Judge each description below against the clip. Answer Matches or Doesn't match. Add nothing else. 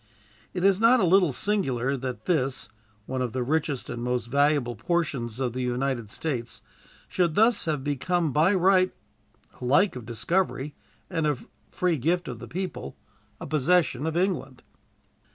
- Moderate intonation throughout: Doesn't match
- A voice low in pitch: Doesn't match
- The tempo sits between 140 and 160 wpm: Matches